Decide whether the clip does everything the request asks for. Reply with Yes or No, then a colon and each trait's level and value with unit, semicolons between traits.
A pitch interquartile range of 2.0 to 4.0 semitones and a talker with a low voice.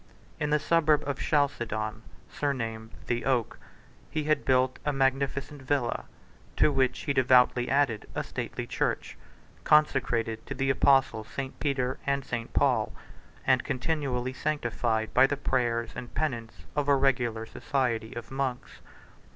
Yes: average, 3.0 semitones; low, 130 Hz